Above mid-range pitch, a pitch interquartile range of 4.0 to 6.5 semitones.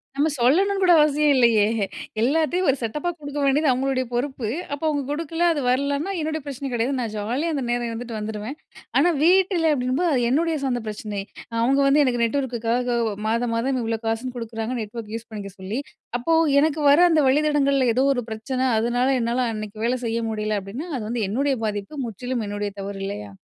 Yes: very high, 250 Hz; average, 4.3 semitones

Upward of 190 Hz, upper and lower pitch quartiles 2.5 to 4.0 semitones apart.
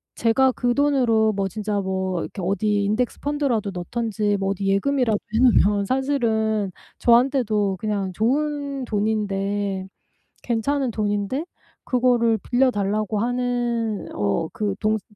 Yes: high, 220 Hz; average, 3.5 semitones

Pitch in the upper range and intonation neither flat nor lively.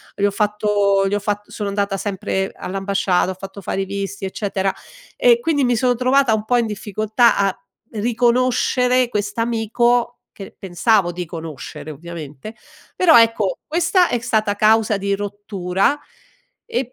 Yes: high, 205 Hz; average, 3.4 semitones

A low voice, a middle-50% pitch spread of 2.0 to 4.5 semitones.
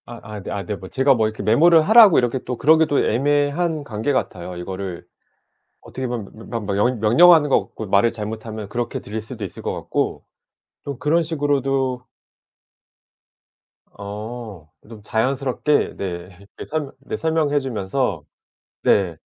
No: low, 120 Hz; wide, 5.5 semitones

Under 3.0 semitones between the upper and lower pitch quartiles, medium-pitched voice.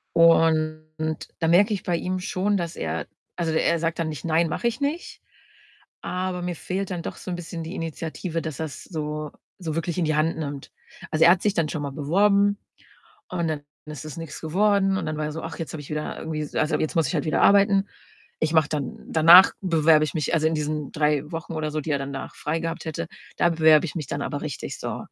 Yes: narrow, 2.5 semitones; medium, 160 Hz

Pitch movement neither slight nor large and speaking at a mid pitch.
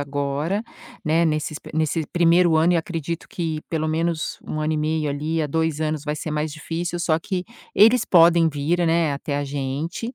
No: narrow, 1.9 semitones; medium, 160 Hz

